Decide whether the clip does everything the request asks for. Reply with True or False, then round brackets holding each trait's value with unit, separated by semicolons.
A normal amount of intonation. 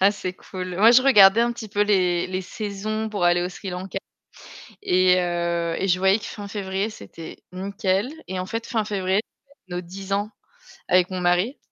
False (2.3 semitones)